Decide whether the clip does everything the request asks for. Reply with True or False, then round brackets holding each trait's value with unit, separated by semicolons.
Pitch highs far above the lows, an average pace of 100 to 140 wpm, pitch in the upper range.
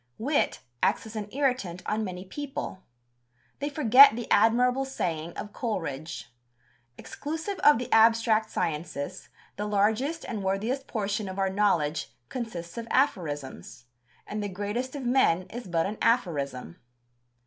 True (5.7 semitones; 135 wpm; 215 Hz)